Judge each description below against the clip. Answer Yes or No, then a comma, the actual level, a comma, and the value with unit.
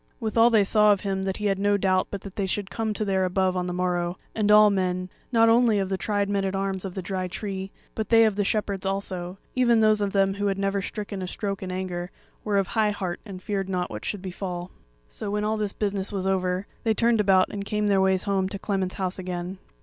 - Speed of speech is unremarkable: No, fast, 250 wpm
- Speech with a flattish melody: Yes, narrow, 1.9 semitones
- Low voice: No, high, 195 Hz